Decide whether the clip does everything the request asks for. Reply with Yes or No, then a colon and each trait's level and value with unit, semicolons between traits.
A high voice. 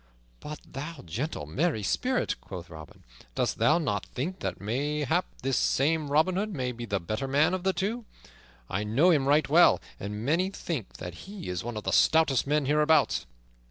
No: medium, 145 Hz